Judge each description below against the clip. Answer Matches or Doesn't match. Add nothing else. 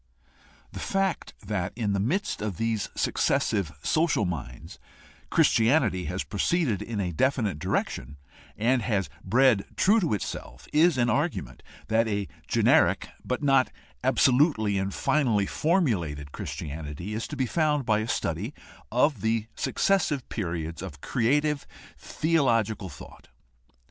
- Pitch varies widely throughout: Matches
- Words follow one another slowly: Matches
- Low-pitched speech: Matches